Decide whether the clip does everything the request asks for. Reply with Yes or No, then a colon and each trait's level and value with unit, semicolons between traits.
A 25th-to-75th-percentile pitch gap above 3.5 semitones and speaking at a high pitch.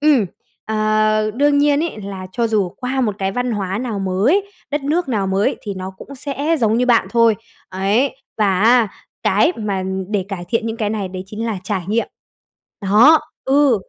Yes: average, 4.9 semitones; high, 220 Hz